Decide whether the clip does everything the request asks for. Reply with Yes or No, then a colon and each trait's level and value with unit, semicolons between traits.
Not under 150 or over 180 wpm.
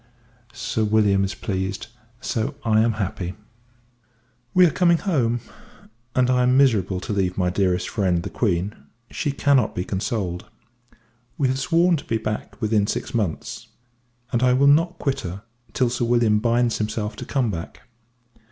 Yes: average, 160 wpm